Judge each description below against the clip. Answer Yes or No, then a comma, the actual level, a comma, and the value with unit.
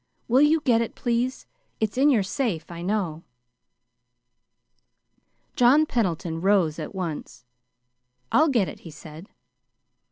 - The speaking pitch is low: No, high, 210 Hz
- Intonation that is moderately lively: No, wide, 7.0 semitones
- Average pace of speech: No, slow, 125 wpm